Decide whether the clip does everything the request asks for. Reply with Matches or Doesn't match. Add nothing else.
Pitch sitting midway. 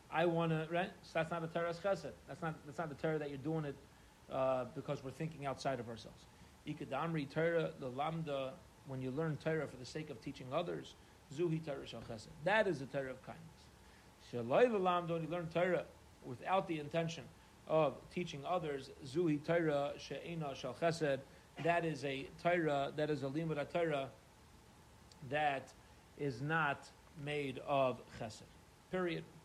Matches